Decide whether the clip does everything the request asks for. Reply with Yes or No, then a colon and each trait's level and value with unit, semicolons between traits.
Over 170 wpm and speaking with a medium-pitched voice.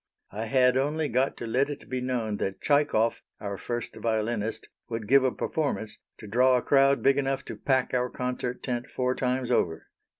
No: average, 190 wpm; low, 125 Hz